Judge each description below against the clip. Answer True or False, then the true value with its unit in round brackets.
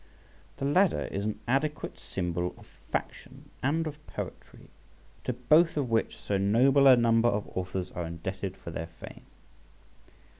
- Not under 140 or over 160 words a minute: True (150 wpm)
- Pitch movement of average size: False (6.8 semitones)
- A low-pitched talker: True (115 Hz)